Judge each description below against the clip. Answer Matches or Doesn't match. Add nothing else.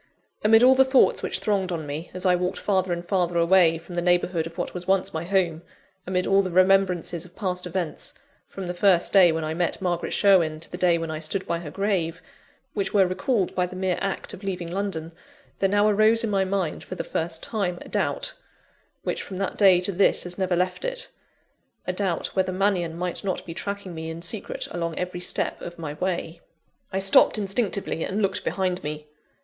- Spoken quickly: Matches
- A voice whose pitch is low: Doesn't match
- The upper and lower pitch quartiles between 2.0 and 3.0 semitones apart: Matches